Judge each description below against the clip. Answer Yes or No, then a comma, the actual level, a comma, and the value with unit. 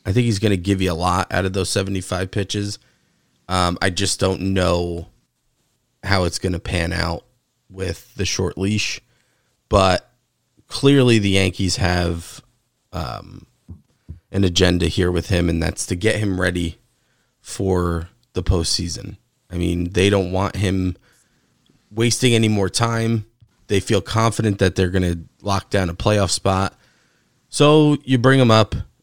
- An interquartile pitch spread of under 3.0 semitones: No, average, 3.8 semitones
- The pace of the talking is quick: No, average, 155 wpm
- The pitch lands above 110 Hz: No, very low, 95 Hz